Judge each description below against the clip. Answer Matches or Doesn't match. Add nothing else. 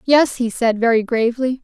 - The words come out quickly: Doesn't match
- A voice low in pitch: Doesn't match